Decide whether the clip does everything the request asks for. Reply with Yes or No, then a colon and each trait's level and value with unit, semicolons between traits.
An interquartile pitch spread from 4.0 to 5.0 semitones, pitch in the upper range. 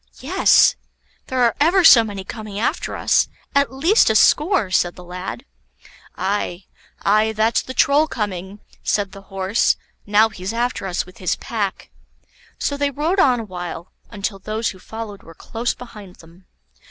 Yes: average, 4.5 semitones; high, 215 Hz